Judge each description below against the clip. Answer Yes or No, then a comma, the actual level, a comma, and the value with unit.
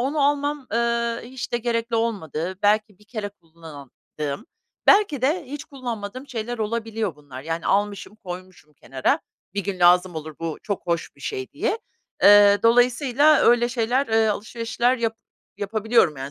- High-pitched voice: Yes, high, 220 Hz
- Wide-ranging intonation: No, average, 4.8 semitones